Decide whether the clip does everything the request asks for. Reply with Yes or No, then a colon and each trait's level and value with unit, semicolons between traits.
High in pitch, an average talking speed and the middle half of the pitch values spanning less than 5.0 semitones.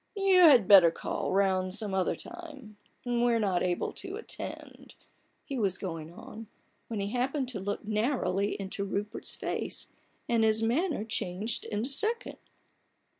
Yes: high, 215 Hz; average, 155 wpm; average, 4.5 semitones